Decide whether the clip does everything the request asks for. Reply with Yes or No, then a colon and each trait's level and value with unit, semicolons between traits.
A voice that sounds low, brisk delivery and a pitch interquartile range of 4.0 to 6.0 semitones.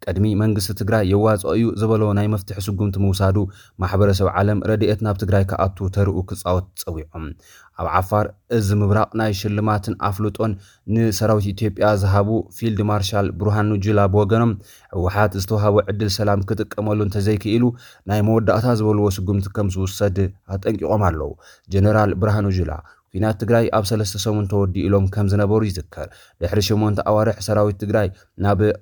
No: low, 105 Hz; fast, 140 wpm; narrow, 1.6 semitones